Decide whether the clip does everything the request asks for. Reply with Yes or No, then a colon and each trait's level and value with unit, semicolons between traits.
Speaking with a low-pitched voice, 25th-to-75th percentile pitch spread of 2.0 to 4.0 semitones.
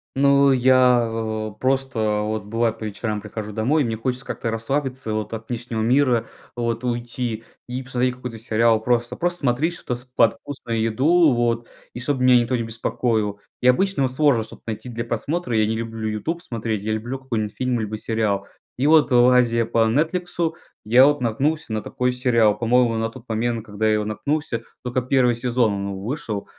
Yes: low, 120 Hz; narrow, 2.5 semitones